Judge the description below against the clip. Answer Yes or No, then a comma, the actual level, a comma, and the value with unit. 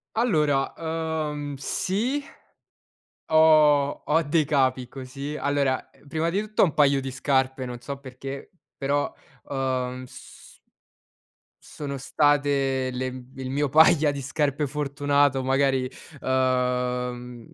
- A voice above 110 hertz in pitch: Yes, medium, 140 Hz